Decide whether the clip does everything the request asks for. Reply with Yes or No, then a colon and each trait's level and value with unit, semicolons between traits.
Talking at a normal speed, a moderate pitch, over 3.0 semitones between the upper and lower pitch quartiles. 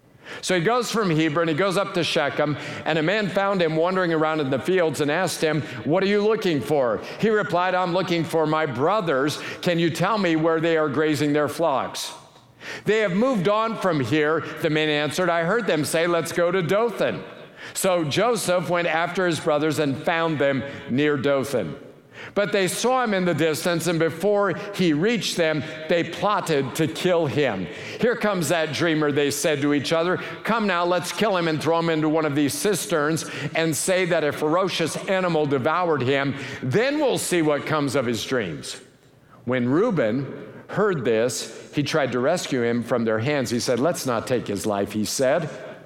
Yes: average, 195 wpm; medium, 165 Hz; average, 3.8 semitones